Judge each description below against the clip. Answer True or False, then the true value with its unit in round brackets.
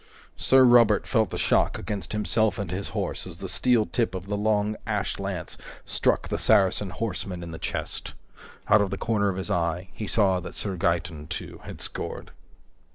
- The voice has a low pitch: True (100 Hz)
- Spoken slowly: False (190 wpm)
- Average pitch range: True (3.0 semitones)